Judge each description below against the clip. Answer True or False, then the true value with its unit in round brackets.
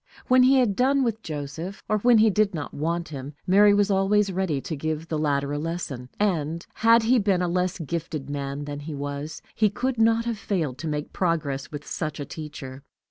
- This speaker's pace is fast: True (210 wpm)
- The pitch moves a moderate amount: False (6.1 semitones)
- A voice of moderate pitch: True (170 Hz)